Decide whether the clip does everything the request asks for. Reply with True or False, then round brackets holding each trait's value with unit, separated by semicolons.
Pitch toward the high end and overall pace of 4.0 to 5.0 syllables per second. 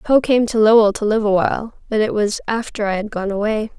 False (215 Hz; 5.8 syllables/s)